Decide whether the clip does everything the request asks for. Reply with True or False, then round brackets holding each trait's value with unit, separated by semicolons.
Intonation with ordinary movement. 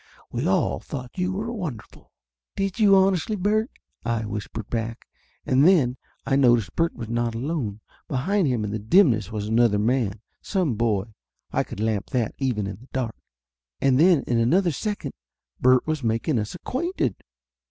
False (8.1 semitones)